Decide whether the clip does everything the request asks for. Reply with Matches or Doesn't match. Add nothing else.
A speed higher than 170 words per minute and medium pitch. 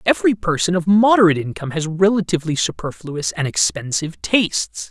Doesn't match